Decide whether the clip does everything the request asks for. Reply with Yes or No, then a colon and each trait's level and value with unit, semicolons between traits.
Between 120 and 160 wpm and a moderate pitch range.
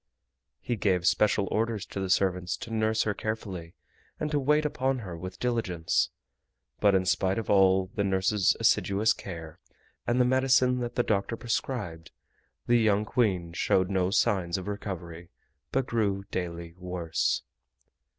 Yes: average, 150 wpm; average, 4.0 semitones